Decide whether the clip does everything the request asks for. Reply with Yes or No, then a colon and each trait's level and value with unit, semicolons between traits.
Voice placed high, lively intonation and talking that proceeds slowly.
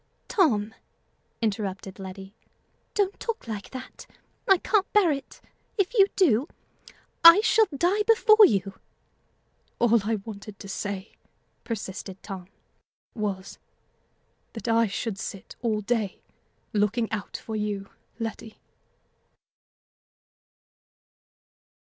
Yes: high, 220 Hz; wide, 8.9 semitones; slow, 105 wpm